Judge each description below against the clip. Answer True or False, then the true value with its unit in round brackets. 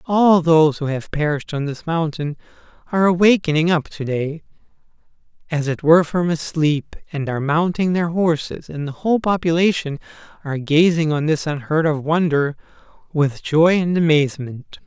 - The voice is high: False (160 Hz)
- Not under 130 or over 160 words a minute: True (155 wpm)